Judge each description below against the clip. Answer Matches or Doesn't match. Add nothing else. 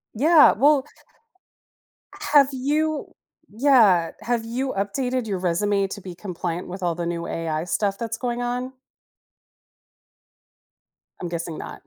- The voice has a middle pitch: Doesn't match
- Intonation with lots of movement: Matches